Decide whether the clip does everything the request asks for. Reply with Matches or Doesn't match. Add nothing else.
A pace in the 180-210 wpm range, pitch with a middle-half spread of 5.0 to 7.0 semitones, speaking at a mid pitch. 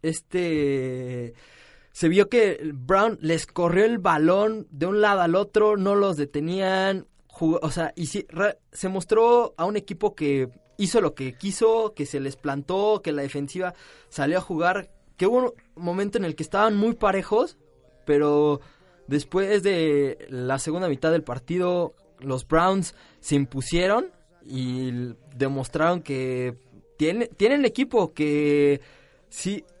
Doesn't match